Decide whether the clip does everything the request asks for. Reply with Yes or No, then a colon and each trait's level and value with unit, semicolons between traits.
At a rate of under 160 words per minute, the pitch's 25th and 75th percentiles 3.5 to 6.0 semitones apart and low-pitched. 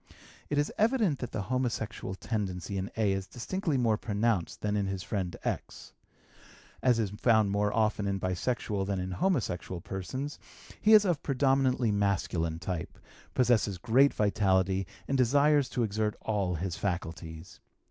Yes: average, 150 wpm; average, 5.1 semitones; low, 105 Hz